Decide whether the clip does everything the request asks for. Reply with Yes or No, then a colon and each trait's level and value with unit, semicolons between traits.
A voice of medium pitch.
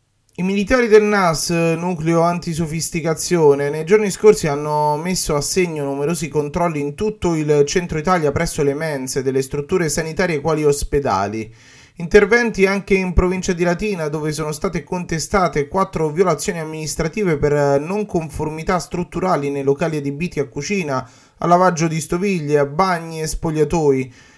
Yes: medium, 160 Hz